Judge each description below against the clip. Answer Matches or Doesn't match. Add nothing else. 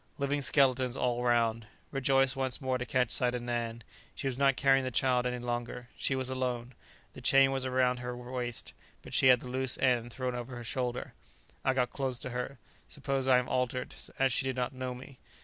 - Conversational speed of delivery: Doesn't match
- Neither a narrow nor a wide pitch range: Doesn't match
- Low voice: Matches